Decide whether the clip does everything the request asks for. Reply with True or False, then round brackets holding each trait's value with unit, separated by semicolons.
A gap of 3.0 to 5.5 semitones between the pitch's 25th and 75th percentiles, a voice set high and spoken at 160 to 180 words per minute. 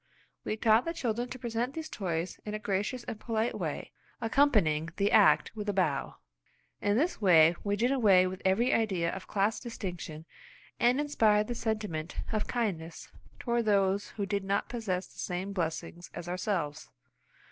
True (4.2 semitones; 205 Hz; 170 wpm)